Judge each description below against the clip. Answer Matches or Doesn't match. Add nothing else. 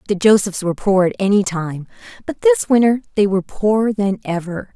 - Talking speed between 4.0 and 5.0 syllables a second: Doesn't match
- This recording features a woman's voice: Matches